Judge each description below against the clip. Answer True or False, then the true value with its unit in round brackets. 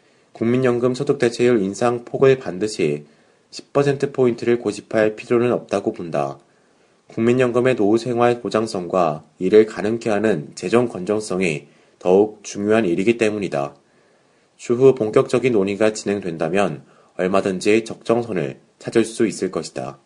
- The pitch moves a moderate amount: True (3.5 semitones)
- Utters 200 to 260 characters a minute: False (295 characters per minute)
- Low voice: True (110 Hz)